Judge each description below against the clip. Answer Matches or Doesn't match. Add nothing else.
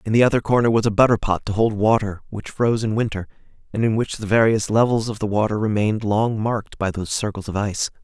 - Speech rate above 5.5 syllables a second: Matches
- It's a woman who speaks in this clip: Doesn't match